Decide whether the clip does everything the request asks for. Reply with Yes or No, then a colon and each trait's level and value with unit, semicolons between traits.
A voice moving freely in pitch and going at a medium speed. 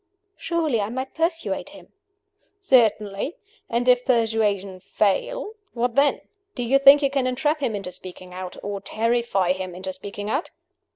Yes: wide, 5.7 semitones; average, 155 wpm